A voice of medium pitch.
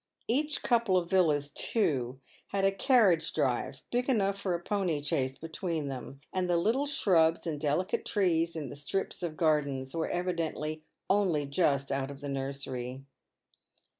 Yes: medium, 165 Hz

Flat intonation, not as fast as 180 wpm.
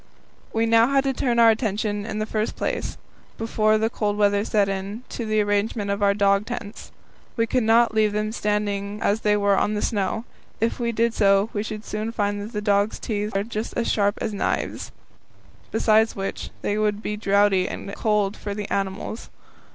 No: narrow, 1.6 semitones; average, 195 wpm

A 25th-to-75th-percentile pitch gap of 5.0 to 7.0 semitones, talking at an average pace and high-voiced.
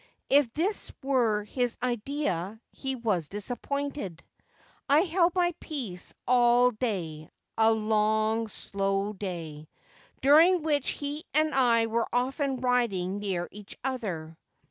No: wide, 5.6 semitones; slow, 125 wpm; high, 235 Hz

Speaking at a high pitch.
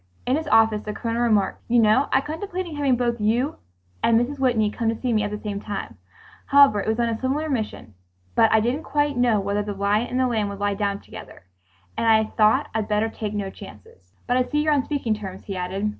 Yes: high, 225 Hz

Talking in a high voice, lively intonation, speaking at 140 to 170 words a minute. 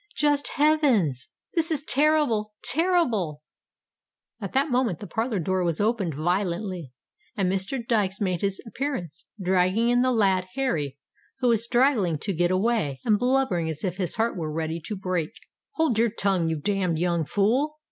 Yes: high, 200 Hz; wide, 5.9 semitones; average, 160 wpm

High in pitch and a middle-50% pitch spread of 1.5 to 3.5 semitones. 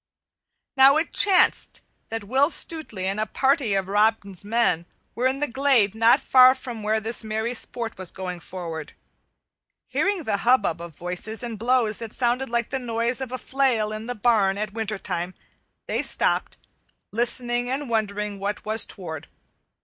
No: high, 225 Hz; average, 3.9 semitones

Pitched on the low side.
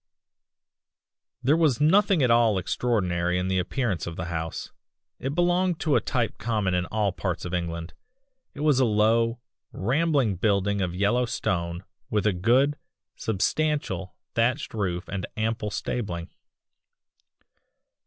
Yes: low, 110 Hz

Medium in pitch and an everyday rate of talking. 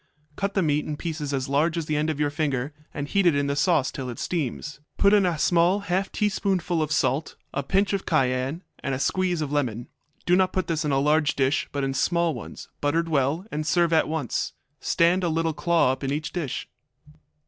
No: medium, 155 Hz; fast, 225 wpm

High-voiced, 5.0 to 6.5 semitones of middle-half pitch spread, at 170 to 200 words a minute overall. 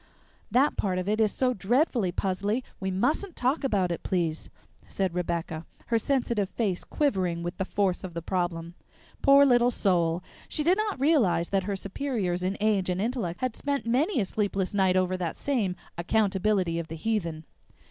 Yes: high, 195 Hz; wide, 5.4 semitones; average, 180 wpm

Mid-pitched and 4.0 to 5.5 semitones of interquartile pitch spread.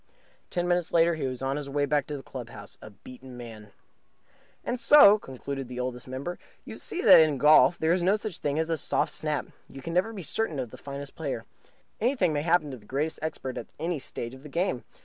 Yes: medium, 150 Hz; average, 4.8 semitones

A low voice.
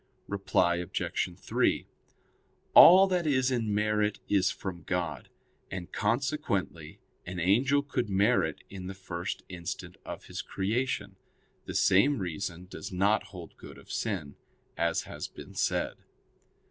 Yes: low, 100 Hz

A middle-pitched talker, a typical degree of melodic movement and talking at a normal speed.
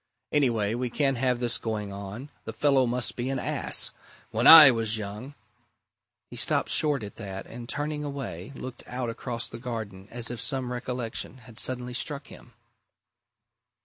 No: low, 120 Hz; average, 3.0 semitones; average, 170 wpm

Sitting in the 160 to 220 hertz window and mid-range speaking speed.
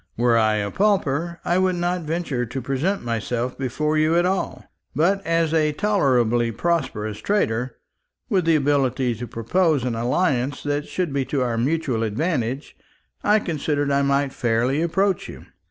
No: medium, 145 Hz; average, 160 wpm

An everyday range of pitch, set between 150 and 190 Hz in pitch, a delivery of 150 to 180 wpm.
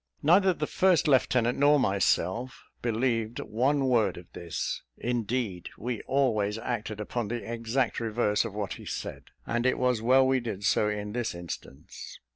No: average, 3.5 semitones; low, 120 Hz; average, 160 wpm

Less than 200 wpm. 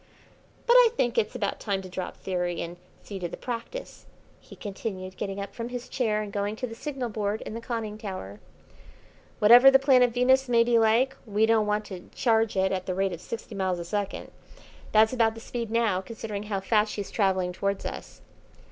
No: fast, 205 wpm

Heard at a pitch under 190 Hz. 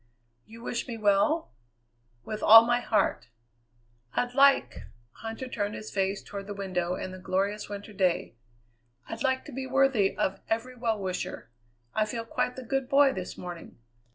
No: high, 220 Hz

